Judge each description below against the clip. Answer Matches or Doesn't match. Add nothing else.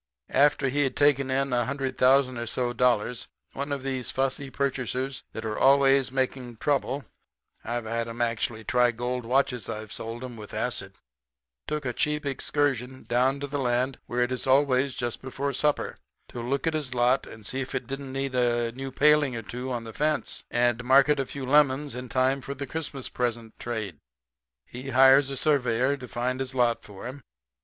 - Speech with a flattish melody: Matches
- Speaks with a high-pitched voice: Doesn't match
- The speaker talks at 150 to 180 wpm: Doesn't match